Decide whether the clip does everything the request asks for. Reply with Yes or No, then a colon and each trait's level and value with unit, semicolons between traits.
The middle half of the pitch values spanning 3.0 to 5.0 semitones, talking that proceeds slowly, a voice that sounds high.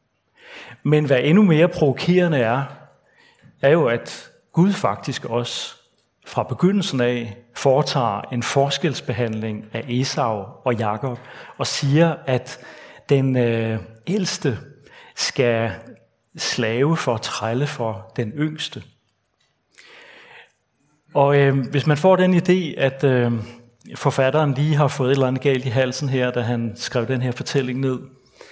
No: average, 3.8 semitones; slow, 135 wpm; low, 135 Hz